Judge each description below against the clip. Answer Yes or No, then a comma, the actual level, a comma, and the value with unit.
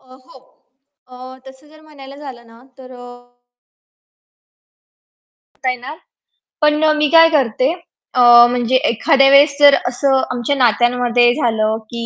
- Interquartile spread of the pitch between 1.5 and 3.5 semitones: Yes, average, 2.8 semitones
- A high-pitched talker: Yes, very high, 260 Hz